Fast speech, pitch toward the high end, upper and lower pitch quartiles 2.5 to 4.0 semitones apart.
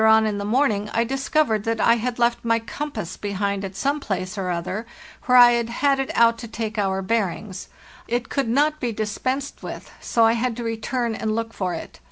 Yes: fast, 220 wpm; high, 230 Hz; average, 2.8 semitones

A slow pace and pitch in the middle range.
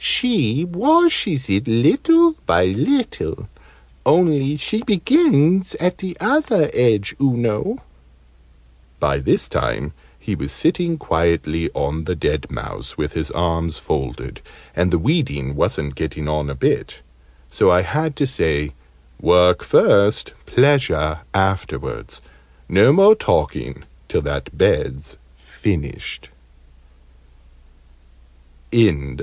No: slow, 110 wpm; low, 105 Hz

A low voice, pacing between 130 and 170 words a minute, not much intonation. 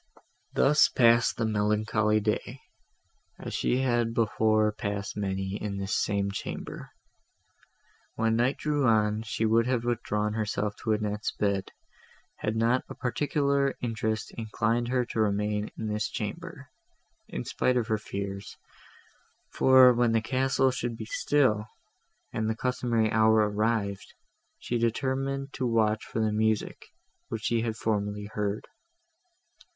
Yes: low, 110 Hz; slow, 135 wpm; narrow, 2.3 semitones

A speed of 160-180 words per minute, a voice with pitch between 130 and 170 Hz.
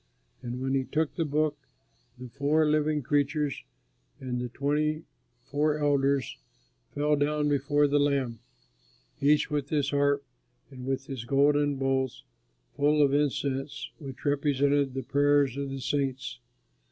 No: average, 140 wpm; medium, 140 Hz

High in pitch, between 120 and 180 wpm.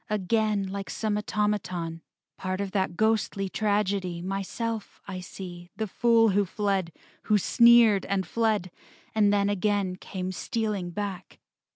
Yes: high, 200 Hz; slow, 135 wpm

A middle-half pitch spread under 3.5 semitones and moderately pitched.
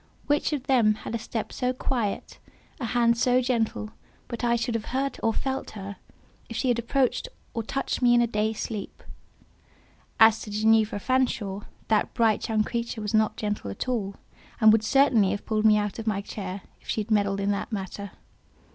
No: narrow, 2.5 semitones; high, 220 Hz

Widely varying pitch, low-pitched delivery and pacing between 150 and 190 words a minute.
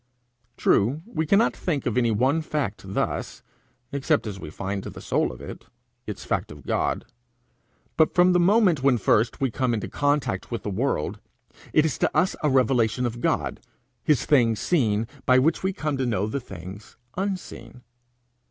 Yes: wide, 5.9 semitones; low, 130 Hz; average, 175 wpm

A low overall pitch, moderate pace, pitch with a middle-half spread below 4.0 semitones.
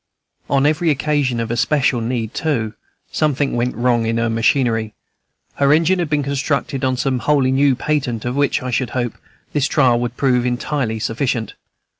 Yes: low, 130 Hz; average, 165 wpm; average, 3.3 semitones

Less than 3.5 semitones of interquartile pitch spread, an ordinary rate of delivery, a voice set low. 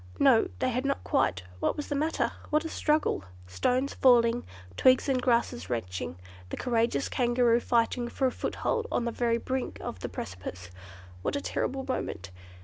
No: average, 2.9 semitones; average, 170 wpm; high, 240 Hz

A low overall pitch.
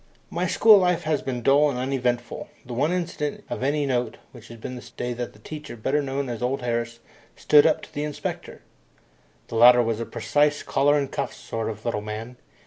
Yes: low, 125 Hz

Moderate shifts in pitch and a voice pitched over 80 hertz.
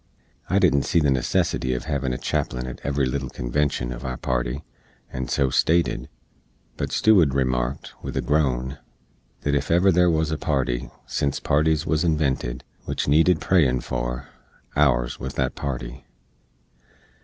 No: average, 3.5 semitones; very low, 70 Hz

